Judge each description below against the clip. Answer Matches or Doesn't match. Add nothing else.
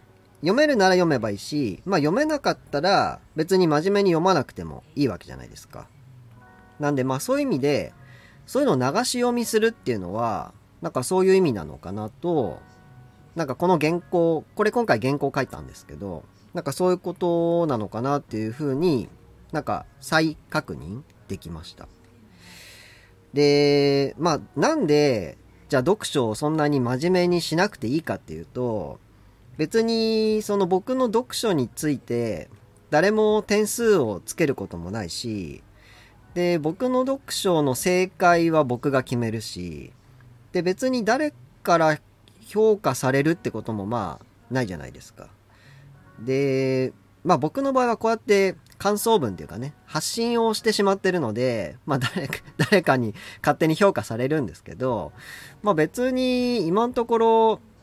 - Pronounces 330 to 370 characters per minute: Doesn't match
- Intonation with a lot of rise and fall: Matches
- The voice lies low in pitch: Doesn't match